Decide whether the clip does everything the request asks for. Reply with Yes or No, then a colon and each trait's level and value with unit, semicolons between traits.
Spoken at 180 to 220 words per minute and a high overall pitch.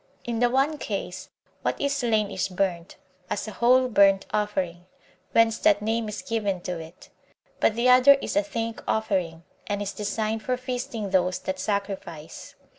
No: average, 170 wpm; high, 210 Hz